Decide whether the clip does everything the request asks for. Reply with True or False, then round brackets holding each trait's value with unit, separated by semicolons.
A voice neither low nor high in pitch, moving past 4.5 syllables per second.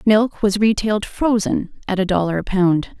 False (205 Hz; 4.7 syllables/s)